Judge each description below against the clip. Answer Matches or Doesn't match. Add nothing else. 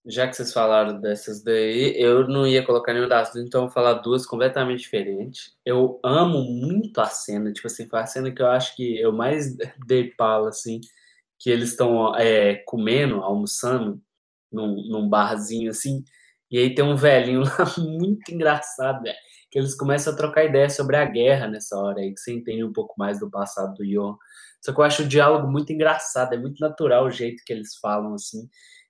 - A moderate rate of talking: Doesn't match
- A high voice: Doesn't match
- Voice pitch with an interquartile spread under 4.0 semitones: Doesn't match